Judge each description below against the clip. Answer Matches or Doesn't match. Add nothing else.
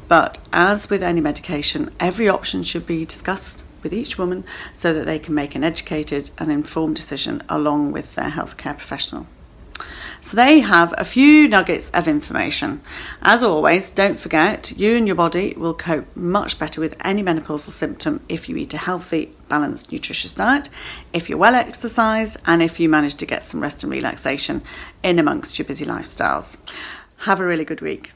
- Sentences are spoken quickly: Doesn't match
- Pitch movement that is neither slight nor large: Matches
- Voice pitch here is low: Doesn't match